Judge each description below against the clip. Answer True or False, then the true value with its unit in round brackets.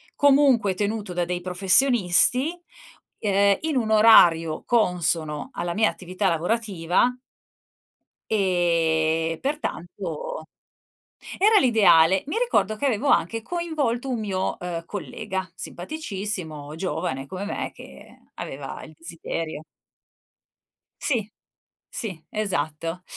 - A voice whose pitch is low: False (190 Hz)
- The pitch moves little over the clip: False (5.4 semitones)